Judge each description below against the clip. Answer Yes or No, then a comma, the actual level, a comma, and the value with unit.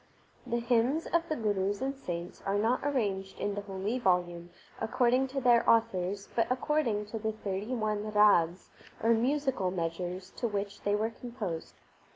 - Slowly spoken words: No, average, 165 wpm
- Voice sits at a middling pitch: No, high, 215 Hz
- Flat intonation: No, average, 4.1 semitones